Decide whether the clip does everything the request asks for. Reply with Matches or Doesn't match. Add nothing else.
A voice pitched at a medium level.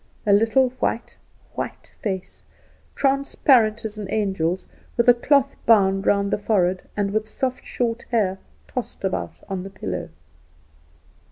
Doesn't match